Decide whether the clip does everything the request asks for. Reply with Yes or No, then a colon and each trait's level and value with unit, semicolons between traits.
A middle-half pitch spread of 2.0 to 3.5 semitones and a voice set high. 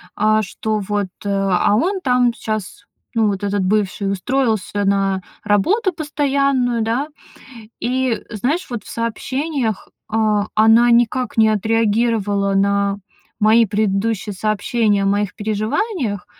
Yes: average, 3.1 semitones; high, 215 Hz